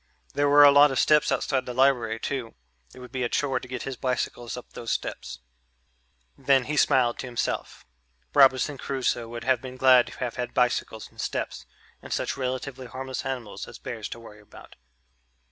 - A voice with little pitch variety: Yes, narrow, 1.9 semitones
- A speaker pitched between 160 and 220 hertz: No, low, 130 Hz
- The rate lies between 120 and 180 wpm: No, average, 190 wpm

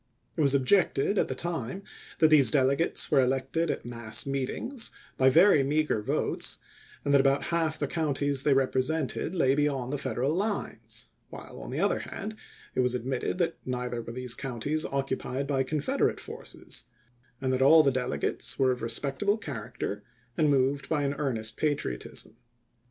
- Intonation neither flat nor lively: Yes, average, 3.1 semitones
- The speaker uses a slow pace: No, average, 170 wpm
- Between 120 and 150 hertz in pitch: Yes, low, 135 Hz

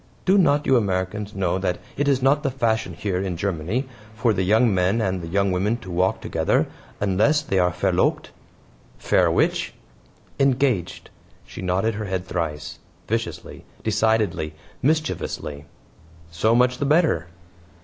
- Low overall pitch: Yes, low, 100 Hz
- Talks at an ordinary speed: Yes, average, 150 wpm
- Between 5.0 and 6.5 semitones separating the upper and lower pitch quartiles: Yes, wide, 5.5 semitones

